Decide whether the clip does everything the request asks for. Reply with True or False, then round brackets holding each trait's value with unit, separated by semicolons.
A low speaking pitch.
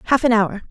False (225 Hz)